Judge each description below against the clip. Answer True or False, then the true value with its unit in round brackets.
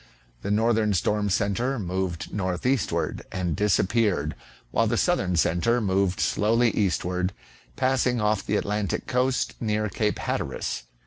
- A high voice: False (105 Hz)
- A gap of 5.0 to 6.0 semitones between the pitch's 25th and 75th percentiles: False (3.7 semitones)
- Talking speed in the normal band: False (130 wpm)